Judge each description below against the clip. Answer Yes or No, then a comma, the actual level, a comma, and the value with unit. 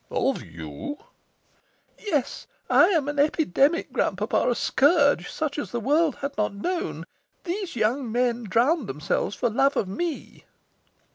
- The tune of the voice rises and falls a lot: Yes, wide, 6.0 semitones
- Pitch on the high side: Yes, very high, 275 Hz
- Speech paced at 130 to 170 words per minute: Yes, average, 145 wpm